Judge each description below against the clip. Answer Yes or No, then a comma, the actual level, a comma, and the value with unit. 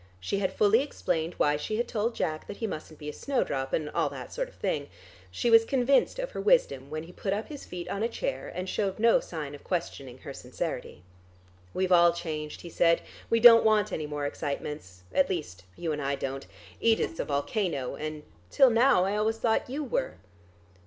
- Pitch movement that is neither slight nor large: No, wide, 7.4 semitones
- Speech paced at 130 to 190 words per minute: No, fast, 205 wpm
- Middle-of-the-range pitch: Yes, medium, 180 Hz